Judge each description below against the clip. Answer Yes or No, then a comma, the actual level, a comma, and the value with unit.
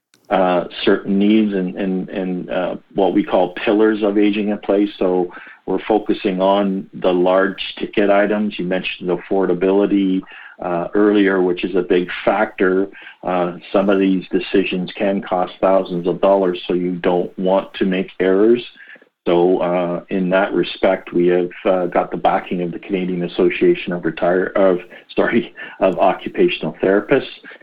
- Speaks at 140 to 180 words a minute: Yes, average, 160 wpm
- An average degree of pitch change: No, narrow, 1.9 semitones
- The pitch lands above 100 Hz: No, very low, 95 Hz